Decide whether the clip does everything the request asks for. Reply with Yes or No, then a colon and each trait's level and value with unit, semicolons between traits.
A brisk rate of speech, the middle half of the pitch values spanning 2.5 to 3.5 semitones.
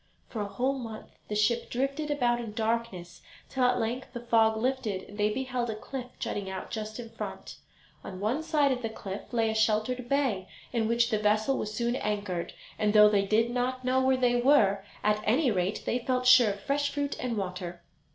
Yes: fast, 210 wpm; average, 3.2 semitones